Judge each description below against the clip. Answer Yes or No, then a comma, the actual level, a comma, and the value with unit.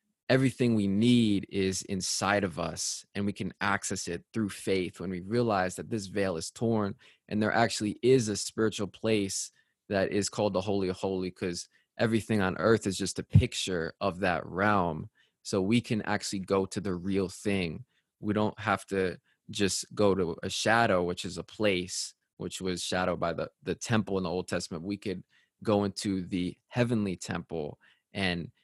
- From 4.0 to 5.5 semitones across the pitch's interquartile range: No, narrow, 2.4 semitones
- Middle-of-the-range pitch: No, low, 100 Hz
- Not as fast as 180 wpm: No, average, 185 wpm